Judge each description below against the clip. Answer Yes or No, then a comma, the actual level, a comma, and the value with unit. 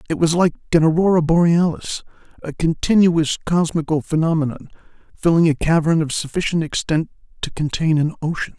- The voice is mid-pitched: Yes, medium, 160 Hz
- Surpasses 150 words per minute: No, average, 140 wpm